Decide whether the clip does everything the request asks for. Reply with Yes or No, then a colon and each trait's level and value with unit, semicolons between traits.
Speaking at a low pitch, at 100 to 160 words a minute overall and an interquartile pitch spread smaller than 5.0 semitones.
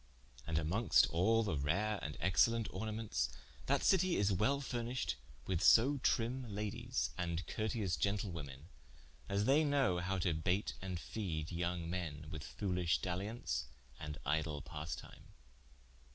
No: very low, 95 Hz; slow, 135 wpm; wide, 5.6 semitones